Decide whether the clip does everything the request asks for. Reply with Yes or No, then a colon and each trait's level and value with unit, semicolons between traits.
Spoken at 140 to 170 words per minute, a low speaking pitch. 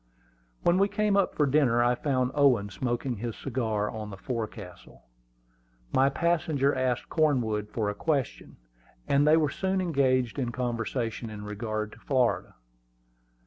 Yes: average, 145 wpm; low, 125 Hz